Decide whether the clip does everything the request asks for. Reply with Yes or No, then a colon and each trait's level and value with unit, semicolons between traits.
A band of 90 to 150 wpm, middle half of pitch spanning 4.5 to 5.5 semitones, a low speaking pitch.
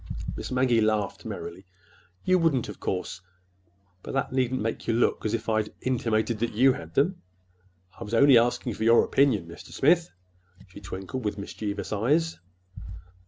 No: average, 160 wpm; average, 4.8 semitones; low, 110 Hz